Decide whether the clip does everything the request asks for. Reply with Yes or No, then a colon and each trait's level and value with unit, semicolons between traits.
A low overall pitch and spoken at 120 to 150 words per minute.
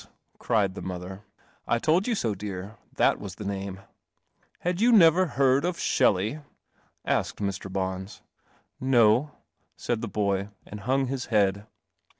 Yes: low, 105 Hz; average, 145 wpm